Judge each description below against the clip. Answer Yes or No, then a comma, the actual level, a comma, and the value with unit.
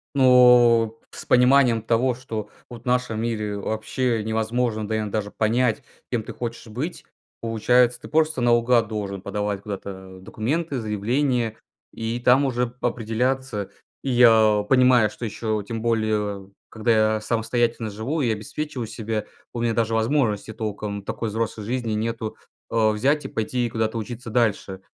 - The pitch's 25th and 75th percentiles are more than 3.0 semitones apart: No, narrow, 2.4 semitones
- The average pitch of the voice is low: Yes, low, 115 Hz